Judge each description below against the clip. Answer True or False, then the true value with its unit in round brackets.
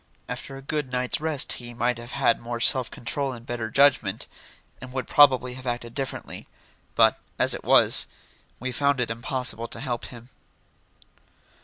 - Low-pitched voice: True (125 Hz)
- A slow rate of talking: False (165 wpm)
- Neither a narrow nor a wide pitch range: False (2.2 semitones)